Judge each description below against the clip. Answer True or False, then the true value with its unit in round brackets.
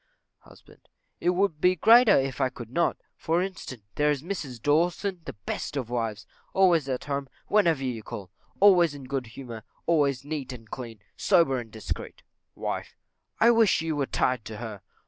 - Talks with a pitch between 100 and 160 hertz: True (140 Hz)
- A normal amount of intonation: False (5.8 semitones)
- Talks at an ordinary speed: True (180 wpm)